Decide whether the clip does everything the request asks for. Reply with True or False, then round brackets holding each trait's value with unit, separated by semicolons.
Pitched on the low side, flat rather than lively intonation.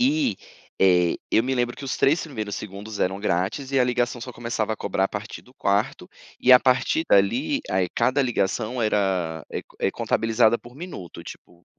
False (115 Hz; 4.6 semitones)